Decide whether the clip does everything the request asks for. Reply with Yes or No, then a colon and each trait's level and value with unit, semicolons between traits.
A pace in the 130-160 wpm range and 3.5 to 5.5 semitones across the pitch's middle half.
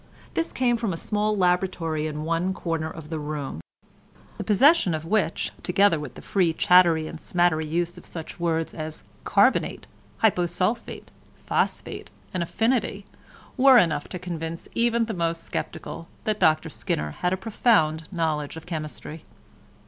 Yes: average, 150 wpm; average, 4.0 semitones